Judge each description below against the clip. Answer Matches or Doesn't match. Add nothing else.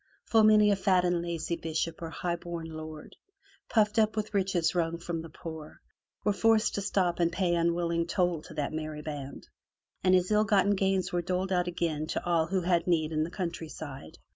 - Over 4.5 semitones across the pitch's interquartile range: Doesn't match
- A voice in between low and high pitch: Matches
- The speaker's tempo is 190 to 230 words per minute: Matches